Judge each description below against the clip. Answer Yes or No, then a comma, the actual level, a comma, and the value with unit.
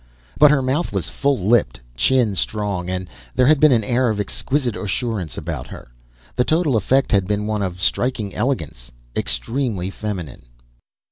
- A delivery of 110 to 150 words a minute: No, average, 160 wpm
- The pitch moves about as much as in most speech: No, wide, 5.9 semitones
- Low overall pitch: Yes, low, 105 Hz